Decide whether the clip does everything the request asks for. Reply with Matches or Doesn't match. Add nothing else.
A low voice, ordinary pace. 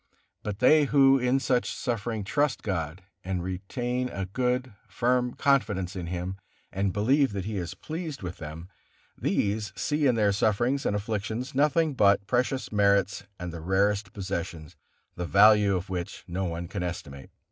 Matches